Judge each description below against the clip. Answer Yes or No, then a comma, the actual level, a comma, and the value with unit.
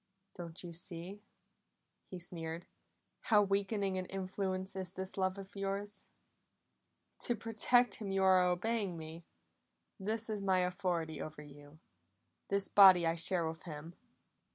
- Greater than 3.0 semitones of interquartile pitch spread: No, average, 2.7 semitones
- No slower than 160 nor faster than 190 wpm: No, slow, 135 wpm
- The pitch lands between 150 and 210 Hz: Yes, medium, 185 Hz